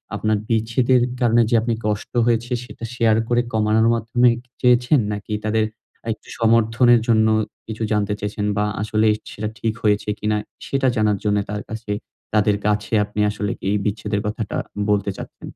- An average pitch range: No, narrow, 1.9 semitones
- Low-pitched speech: Yes, low, 110 Hz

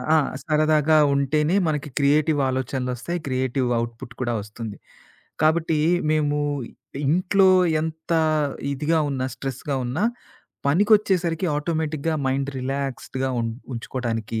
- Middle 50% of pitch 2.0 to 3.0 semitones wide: No, average, 3.6 semitones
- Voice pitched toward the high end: No, medium, 145 Hz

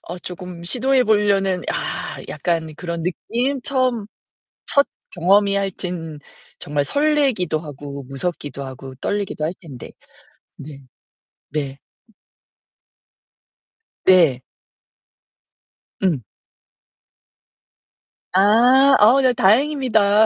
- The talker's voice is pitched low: No, medium, 185 Hz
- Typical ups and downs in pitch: No, wide, 7.0 semitones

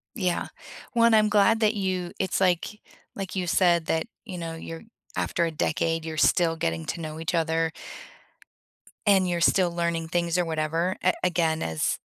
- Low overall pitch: No, medium, 170 Hz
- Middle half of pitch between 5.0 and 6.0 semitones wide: No, narrow, 2.4 semitones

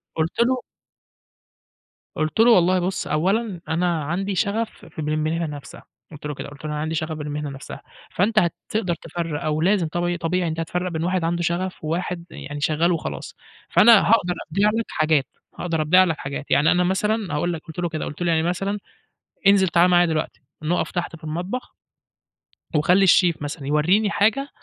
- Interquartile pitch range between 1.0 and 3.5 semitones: Yes, average, 3.1 semitones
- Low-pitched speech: No, medium, 170 Hz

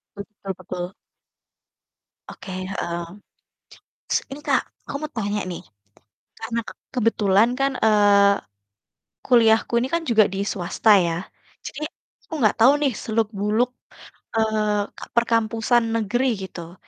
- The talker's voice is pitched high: Yes, high, 215 Hz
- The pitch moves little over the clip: No, average, 3.2 semitones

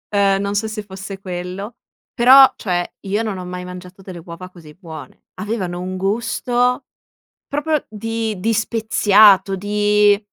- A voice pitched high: Yes, high, 200 Hz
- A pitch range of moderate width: Yes, average, 3.2 semitones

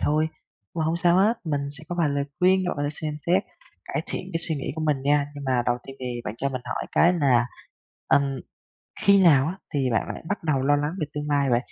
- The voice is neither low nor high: Yes, medium, 145 Hz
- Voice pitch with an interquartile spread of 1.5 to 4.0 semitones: Yes, average, 3.6 semitones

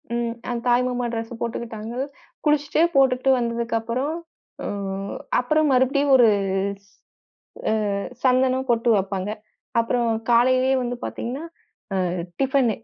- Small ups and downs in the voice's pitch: Yes, narrow, 2.2 semitones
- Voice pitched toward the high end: Yes, high, 245 Hz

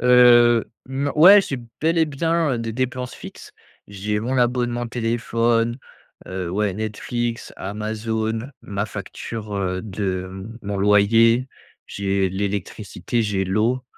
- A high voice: No, low, 115 Hz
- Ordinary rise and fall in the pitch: Yes, average, 3.2 semitones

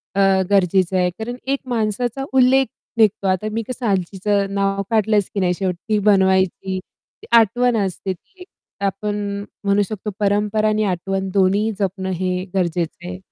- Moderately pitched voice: No, high, 200 Hz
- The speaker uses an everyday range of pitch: No, narrow, 2.3 semitones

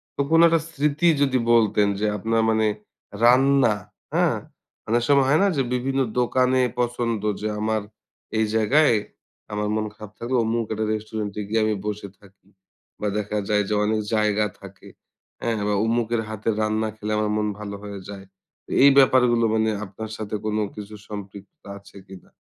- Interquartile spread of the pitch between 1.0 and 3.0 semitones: Yes, narrow, 2.5 semitones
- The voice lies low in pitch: Yes, low, 110 Hz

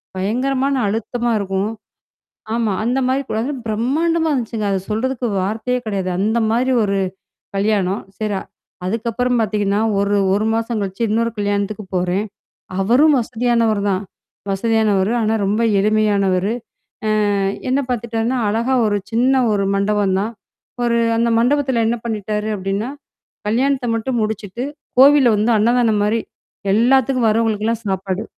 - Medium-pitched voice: No, high, 220 Hz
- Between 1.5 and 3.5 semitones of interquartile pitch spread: Yes, average, 2.9 semitones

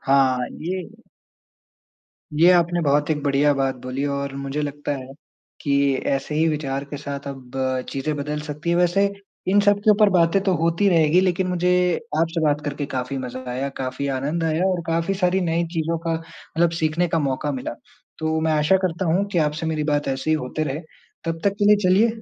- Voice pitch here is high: No, medium, 155 Hz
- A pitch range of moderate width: Yes, average, 3.7 semitones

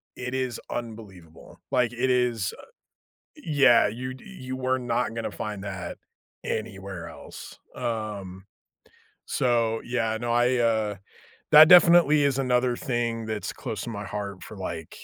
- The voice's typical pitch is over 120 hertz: No, low, 115 Hz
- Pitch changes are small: No, average, 3.5 semitones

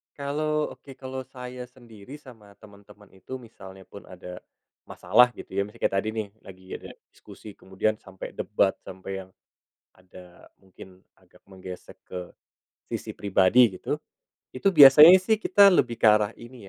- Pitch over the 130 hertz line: No, low, 105 Hz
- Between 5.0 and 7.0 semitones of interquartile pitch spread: Yes, wide, 5.4 semitones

